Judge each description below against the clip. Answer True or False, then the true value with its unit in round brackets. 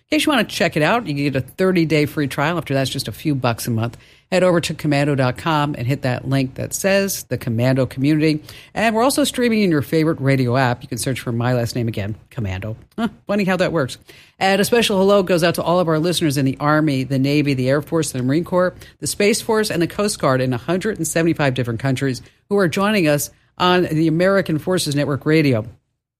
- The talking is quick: True (235 wpm)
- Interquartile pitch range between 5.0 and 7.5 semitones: True (5.5 semitones)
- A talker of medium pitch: True (150 Hz)